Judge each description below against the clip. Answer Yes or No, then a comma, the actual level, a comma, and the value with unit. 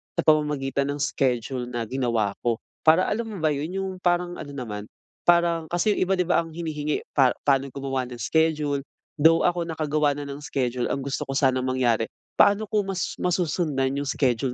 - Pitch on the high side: No, medium, 145 Hz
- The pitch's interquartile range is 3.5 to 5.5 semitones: Yes, average, 4.4 semitones